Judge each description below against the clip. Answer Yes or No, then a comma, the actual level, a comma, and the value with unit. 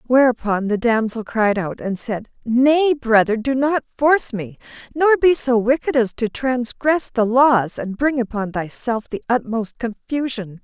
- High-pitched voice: Yes, high, 240 Hz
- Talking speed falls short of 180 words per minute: Yes, average, 165 wpm